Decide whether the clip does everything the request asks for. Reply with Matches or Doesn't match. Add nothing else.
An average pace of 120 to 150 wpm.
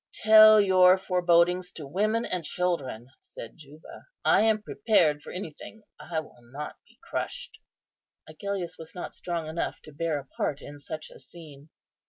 Doesn't match